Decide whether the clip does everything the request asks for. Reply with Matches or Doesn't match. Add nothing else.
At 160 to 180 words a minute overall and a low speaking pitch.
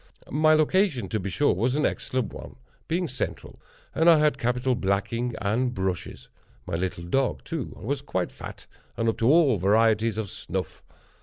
Matches